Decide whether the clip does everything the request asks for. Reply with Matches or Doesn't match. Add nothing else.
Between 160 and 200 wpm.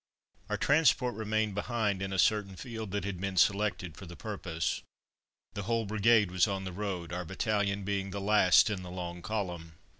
Matches